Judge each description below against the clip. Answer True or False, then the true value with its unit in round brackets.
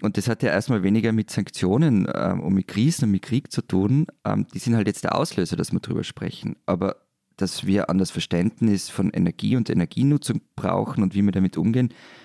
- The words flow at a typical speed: False (205 wpm)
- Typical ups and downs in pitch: True (3.8 semitones)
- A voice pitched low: True (110 Hz)